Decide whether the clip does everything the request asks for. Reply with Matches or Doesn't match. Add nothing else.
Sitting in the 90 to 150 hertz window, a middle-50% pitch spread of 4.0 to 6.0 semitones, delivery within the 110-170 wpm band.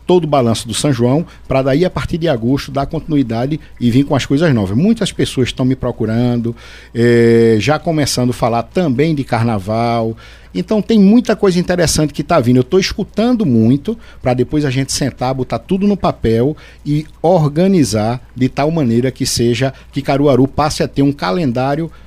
Doesn't match